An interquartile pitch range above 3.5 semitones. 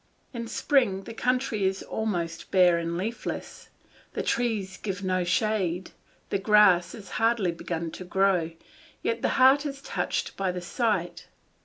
Yes: average, 4.3 semitones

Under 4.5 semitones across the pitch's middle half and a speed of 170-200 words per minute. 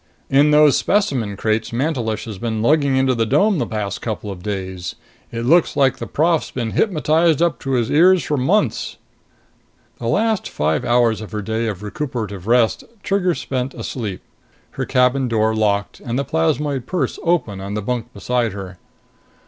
No: wide, 5.6 semitones; average, 175 wpm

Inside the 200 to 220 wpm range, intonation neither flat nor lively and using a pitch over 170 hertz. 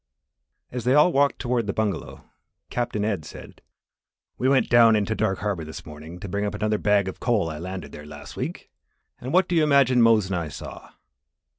No: fast, 205 wpm; average, 4.5 semitones; low, 105 Hz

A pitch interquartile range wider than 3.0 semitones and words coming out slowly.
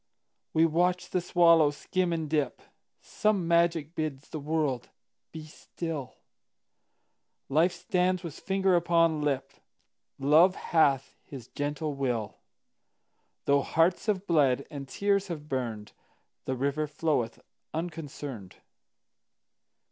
Yes: average, 3.6 semitones; slow, 95 wpm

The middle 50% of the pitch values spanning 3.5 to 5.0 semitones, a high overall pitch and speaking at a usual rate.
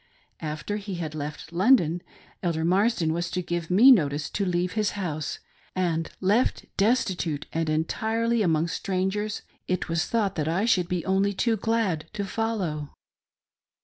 No: average, 4.2 semitones; medium, 180 Hz; average, 150 wpm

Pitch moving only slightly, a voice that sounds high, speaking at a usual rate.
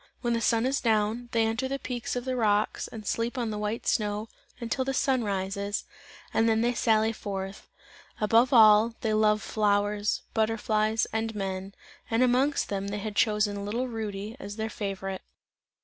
Yes: narrow, 2.1 semitones; high, 220 Hz; average, 175 wpm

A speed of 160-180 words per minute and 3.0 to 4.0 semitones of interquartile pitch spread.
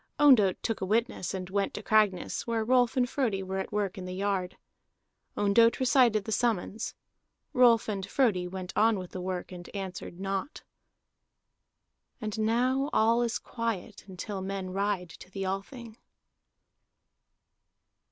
No: average, 145 wpm; average, 3.5 semitones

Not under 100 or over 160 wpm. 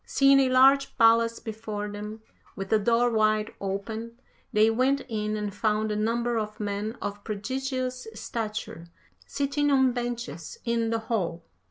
Yes: average, 150 wpm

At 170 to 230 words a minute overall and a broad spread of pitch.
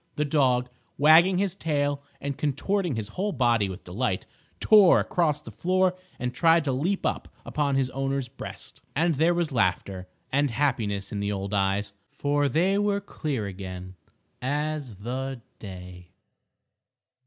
No: average, 150 wpm; wide, 7.4 semitones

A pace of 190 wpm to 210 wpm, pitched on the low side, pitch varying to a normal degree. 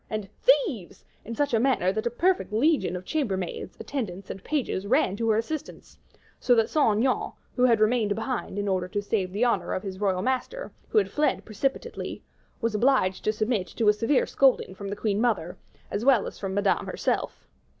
No: average, 200 wpm; high, 220 Hz; average, 4.7 semitones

